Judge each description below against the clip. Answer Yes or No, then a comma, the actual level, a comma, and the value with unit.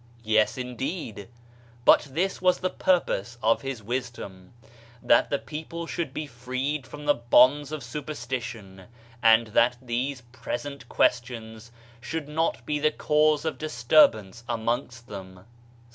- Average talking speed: No, slow, 130 wpm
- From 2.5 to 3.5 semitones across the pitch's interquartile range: No, average, 4.3 semitones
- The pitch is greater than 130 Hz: No, low, 125 Hz